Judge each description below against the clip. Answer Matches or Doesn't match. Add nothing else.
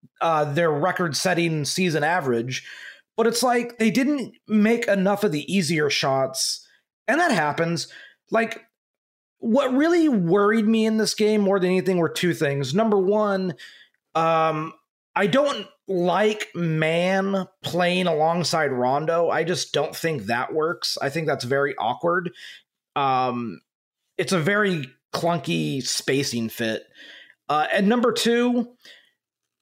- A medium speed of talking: Doesn't match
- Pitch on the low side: Doesn't match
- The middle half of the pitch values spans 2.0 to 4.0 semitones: Doesn't match